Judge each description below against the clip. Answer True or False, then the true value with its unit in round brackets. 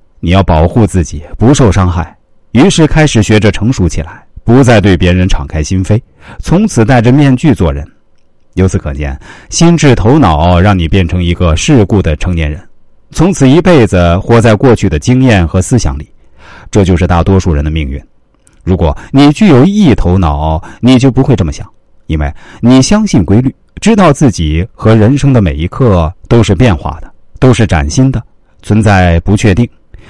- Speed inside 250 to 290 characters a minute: True (260 characters per minute)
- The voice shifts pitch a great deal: True (6.5 semitones)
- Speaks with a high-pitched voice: False (100 Hz)